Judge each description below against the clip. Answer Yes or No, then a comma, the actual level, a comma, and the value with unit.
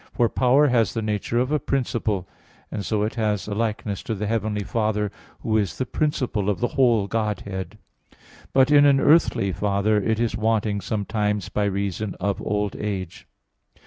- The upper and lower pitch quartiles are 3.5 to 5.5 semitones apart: No, narrow, 2.4 semitones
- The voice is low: Yes, low, 105 Hz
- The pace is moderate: Yes, average, 175 wpm